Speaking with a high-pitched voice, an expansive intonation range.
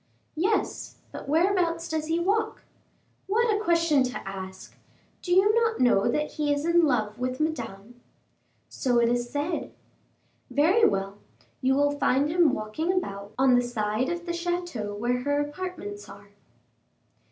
Yes: very high, 290 Hz; wide, 6.5 semitones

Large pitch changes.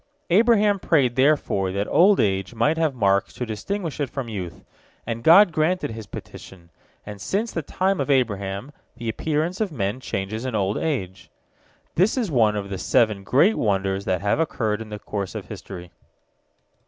Yes: wide, 8.4 semitones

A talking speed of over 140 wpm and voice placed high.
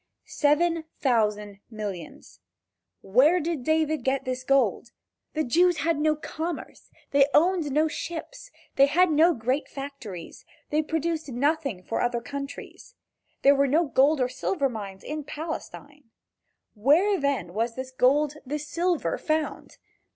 No: slow, 135 wpm; very high, 285 Hz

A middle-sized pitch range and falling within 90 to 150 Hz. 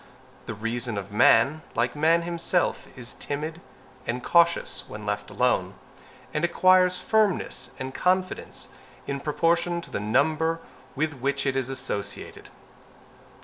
No: wide, 6.0 semitones; medium, 140 Hz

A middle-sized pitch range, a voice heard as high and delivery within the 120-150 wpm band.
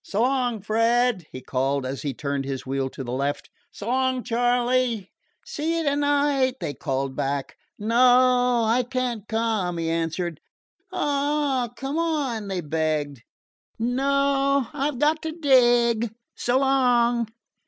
No: wide, 8.1 semitones; high, 240 Hz; average, 140 wpm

